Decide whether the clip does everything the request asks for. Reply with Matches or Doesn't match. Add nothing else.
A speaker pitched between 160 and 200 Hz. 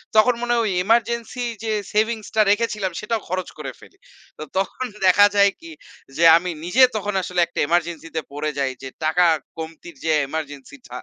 Matches